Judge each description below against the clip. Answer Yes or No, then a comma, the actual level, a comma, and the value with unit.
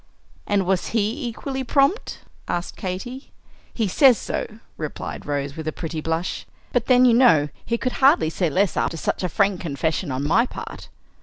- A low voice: No, high, 195 Hz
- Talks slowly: No, average, 175 wpm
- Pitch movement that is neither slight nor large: No, wide, 7.2 semitones